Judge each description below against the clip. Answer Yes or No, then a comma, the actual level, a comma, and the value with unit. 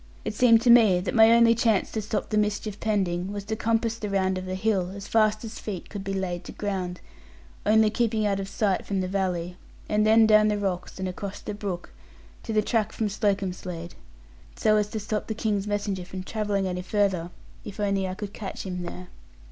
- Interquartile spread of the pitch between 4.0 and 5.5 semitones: No, narrow, 2.4 semitones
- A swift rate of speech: Yes, fast, 215 wpm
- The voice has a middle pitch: No, high, 205 Hz